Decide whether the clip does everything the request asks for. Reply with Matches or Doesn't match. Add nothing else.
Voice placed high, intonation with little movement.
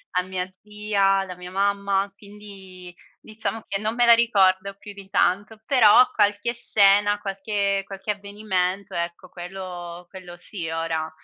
Matches